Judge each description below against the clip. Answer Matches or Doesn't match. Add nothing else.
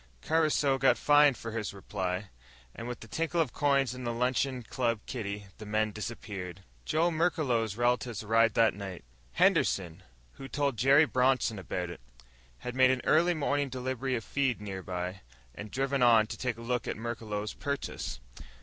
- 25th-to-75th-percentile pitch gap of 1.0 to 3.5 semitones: Doesn't match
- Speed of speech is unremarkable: Matches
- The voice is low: Matches